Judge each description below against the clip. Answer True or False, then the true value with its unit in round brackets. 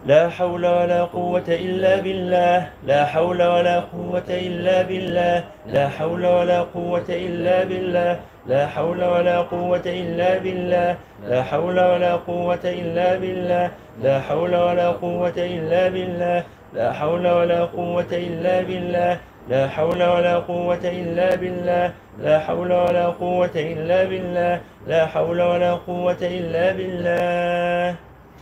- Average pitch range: False (0.5 semitones)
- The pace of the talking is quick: False (125 wpm)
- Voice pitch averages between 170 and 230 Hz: True (175 Hz)